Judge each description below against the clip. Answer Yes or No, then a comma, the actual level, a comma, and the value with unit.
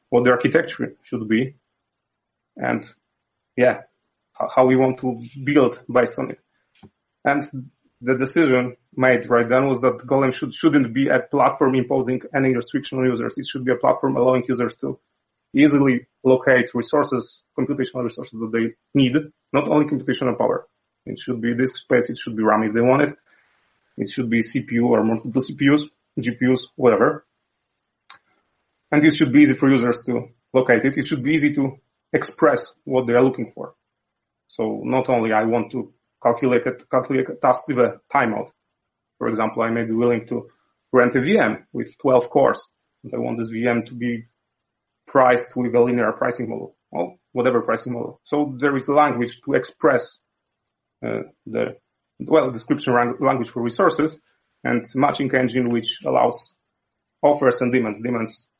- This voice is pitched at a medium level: No, low, 125 Hz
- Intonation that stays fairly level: Yes, narrow, 2.2 semitones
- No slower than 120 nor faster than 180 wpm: Yes, average, 170 wpm